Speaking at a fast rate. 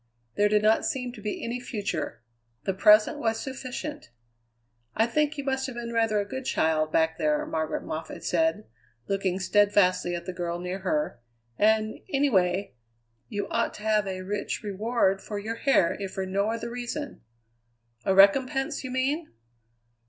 No: average, 165 wpm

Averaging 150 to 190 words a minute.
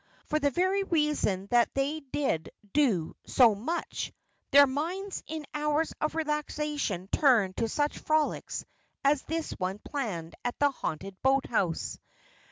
No: slow, 135 wpm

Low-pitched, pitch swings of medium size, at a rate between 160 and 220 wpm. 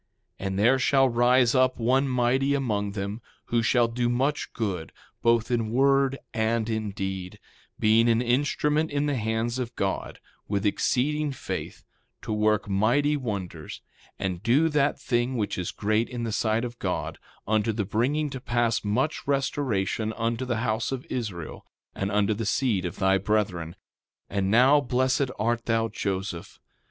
Yes: low, 115 Hz; average, 3.8 semitones; average, 165 wpm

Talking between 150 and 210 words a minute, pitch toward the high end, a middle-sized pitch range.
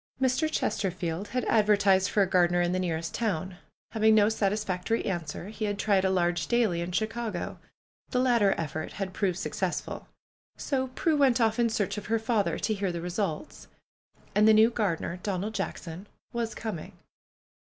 Yes: average, 175 wpm; high, 205 Hz; average, 3.8 semitones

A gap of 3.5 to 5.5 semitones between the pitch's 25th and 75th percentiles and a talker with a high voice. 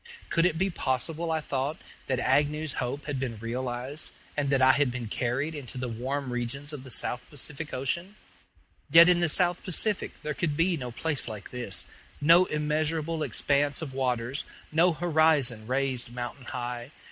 No: average, 4.1 semitones; medium, 140 Hz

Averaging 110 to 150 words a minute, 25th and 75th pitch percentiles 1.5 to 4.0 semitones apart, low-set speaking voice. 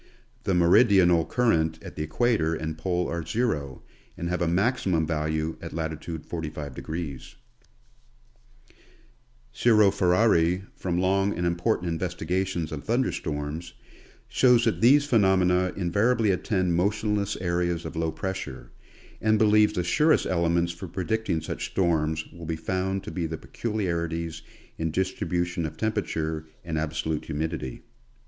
Yes: slow, 135 wpm; average, 3.4 semitones; very low, 85 Hz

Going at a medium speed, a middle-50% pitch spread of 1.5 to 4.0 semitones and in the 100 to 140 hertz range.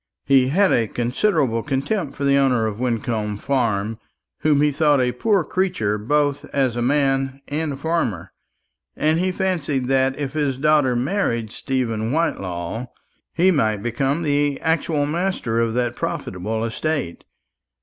No: average, 150 wpm; average, 4.7 semitones; low, 135 Hz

